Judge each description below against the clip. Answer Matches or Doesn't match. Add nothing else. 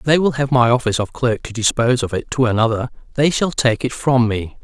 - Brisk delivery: Matches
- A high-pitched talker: Doesn't match